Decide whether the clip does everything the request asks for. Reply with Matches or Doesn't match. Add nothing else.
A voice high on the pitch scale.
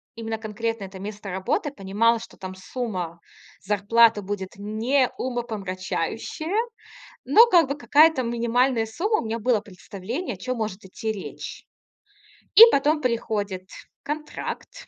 Matches